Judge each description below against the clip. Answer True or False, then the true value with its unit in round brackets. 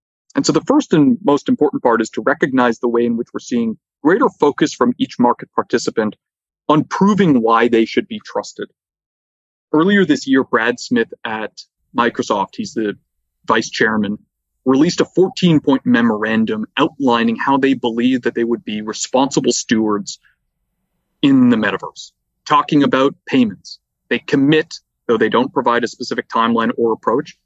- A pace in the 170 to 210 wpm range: False (160 wpm)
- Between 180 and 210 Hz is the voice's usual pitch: False (135 Hz)